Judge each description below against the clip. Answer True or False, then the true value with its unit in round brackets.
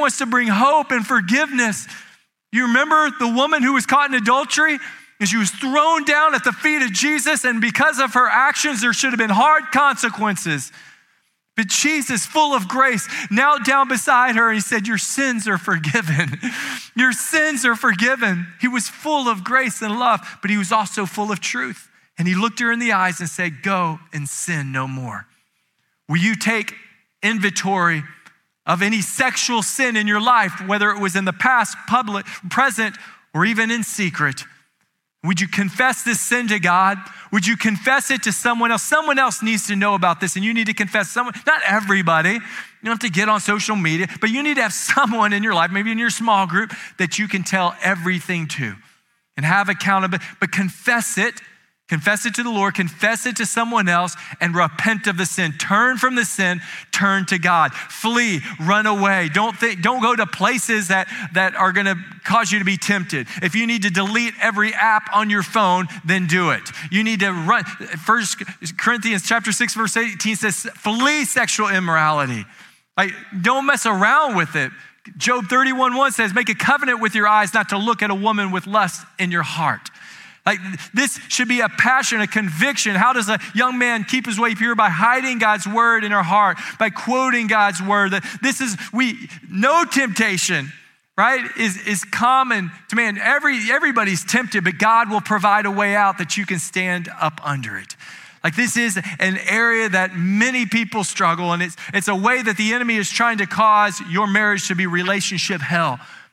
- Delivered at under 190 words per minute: False (195 wpm)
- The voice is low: False (215 Hz)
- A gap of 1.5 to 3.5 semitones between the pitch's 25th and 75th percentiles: False (4.1 semitones)